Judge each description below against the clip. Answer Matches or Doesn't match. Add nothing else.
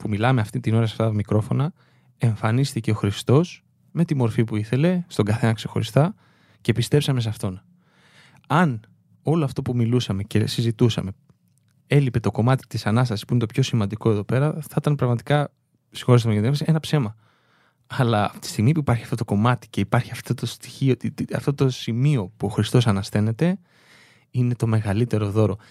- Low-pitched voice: Matches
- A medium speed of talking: Doesn't match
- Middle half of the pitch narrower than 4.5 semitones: Matches